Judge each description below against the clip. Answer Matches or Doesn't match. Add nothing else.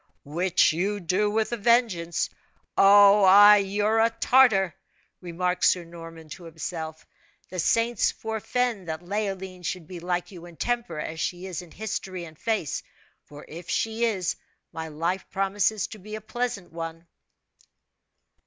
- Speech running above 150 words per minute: Doesn't match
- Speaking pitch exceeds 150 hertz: Matches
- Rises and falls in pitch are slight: Doesn't match